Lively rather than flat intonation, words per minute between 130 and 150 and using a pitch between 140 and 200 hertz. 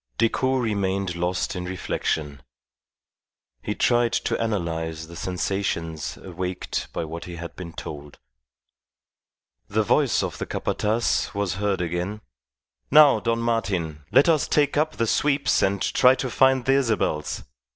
No: wide, 5.7 semitones; average, 140 wpm; very low, 95 Hz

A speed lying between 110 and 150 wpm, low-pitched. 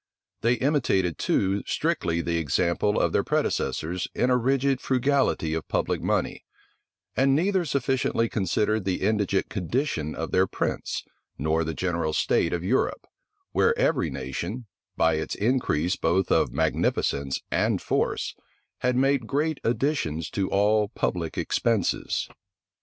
Yes: slow, 135 wpm; low, 100 Hz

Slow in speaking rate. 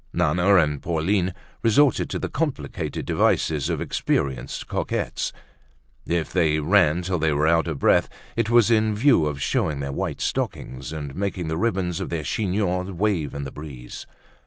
No: average, 165 wpm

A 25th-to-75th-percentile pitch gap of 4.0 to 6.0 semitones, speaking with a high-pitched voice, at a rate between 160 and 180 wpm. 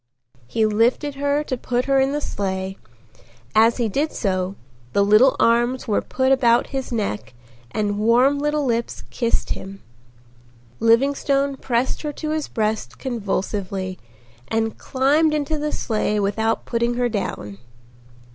No: average, 4.6 semitones; high, 235 Hz; average, 140 wpm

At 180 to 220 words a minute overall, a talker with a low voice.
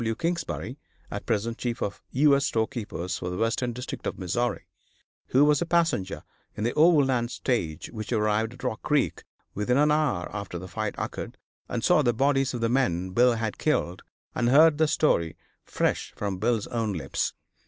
Yes: average, 185 wpm; low, 120 Hz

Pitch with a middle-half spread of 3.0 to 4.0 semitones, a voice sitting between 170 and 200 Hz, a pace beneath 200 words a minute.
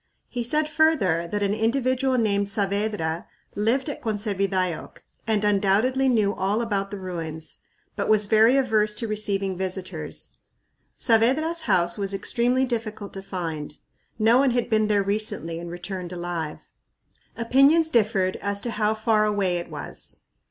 No: average, 3.6 semitones; high, 210 Hz; average, 145 wpm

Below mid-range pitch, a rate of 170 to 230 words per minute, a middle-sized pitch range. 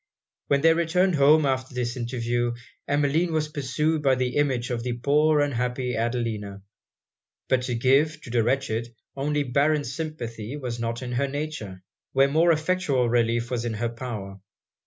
No: low, 130 Hz; average, 160 wpm; average, 3.8 semitones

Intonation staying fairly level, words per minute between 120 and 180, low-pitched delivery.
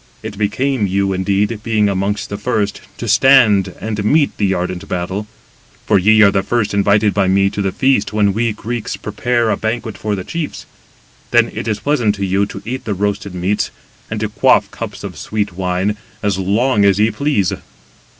No: narrow, 2.1 semitones; average, 190 wpm; low, 105 Hz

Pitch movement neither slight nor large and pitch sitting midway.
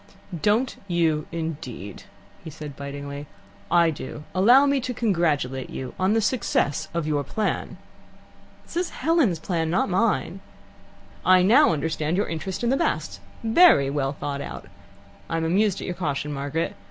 No: wide, 6.1 semitones; medium, 170 Hz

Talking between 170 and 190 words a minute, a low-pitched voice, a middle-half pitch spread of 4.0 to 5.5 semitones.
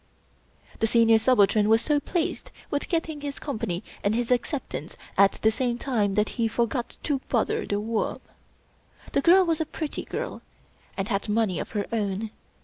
No: average, 175 wpm; high, 230 Hz; average, 4.9 semitones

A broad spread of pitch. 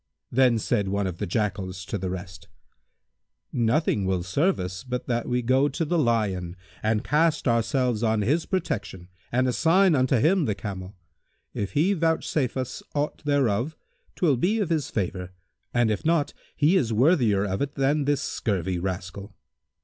Yes: wide, 6.8 semitones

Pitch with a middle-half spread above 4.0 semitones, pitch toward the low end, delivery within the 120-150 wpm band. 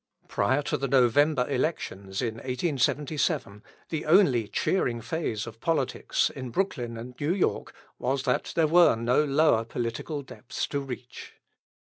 Yes: average, 4.5 semitones; low, 130 Hz; average, 140 wpm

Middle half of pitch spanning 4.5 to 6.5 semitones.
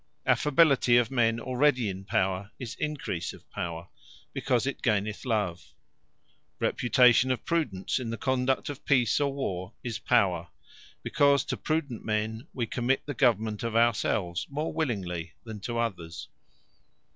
Yes: average, 4.9 semitones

